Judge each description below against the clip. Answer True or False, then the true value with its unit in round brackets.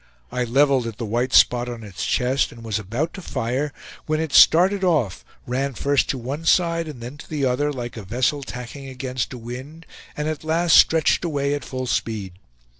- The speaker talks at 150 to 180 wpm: False (200 wpm)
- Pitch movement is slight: False (4.0 semitones)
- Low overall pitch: True (130 Hz)